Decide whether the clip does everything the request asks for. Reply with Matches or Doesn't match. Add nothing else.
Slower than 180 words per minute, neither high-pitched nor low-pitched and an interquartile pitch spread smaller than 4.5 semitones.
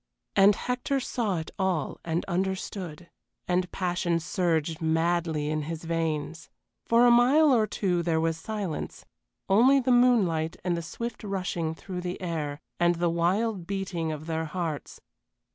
Matches